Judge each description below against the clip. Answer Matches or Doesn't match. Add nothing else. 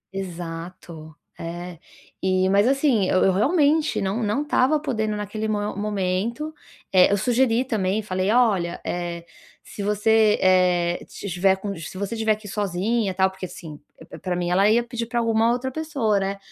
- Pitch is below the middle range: Doesn't match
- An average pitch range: Matches